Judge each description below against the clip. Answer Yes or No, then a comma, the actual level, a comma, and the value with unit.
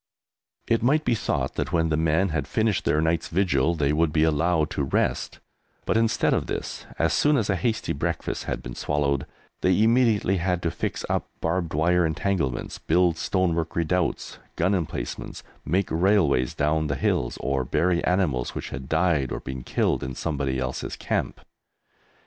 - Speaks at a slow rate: No, average, 170 wpm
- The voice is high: No, very low, 80 Hz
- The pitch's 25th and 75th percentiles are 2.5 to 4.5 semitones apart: Yes, average, 4.0 semitones